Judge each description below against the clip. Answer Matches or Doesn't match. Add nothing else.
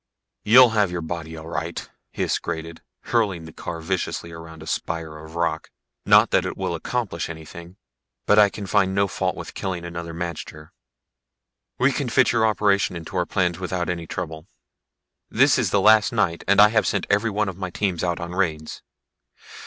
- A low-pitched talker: Matches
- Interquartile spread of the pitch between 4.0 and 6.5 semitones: Doesn't match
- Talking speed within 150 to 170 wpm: Doesn't match